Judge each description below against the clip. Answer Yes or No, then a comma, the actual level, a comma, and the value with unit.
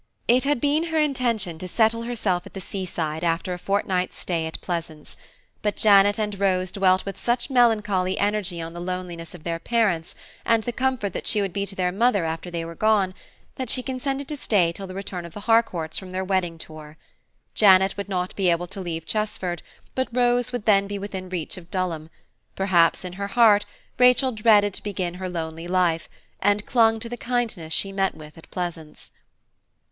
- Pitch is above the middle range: Yes, high, 195 Hz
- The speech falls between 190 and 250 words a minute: Yes, average, 200 wpm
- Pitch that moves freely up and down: No, average, 4.1 semitones